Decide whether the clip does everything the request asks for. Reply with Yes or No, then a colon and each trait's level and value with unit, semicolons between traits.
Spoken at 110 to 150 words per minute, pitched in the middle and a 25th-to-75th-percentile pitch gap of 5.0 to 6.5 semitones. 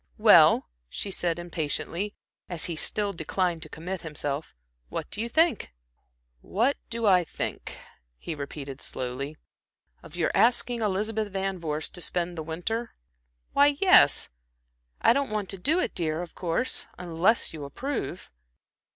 Yes: average, 145 wpm; medium, 180 Hz; wide, 5.4 semitones